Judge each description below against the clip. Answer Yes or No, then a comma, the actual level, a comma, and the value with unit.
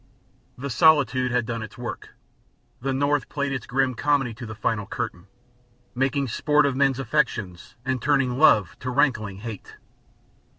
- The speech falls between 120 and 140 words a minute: No, average, 160 wpm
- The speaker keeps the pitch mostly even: No, average, 3.7 semitones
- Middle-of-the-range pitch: No, low, 130 Hz